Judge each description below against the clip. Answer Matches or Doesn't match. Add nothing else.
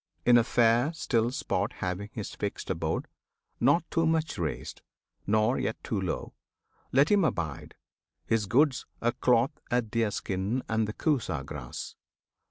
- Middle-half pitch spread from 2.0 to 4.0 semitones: Doesn't match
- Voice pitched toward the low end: Matches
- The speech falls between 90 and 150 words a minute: Matches